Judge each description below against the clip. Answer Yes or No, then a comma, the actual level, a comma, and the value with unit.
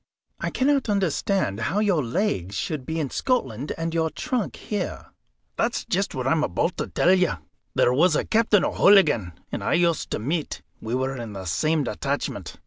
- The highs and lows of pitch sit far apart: Yes, wide, 7.3 semitones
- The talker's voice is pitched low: No, medium, 160 Hz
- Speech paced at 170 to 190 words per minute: Yes, average, 185 wpm